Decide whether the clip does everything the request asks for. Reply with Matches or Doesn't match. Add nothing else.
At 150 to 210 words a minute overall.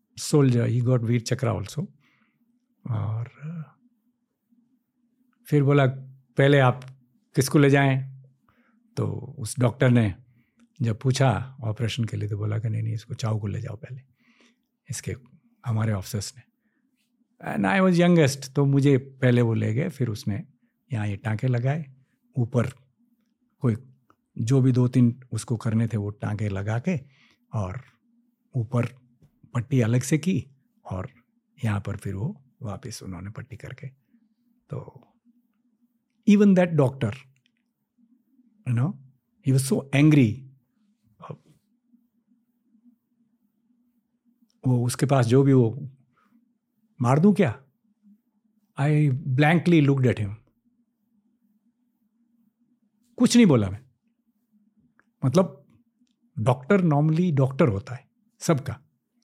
Doesn't match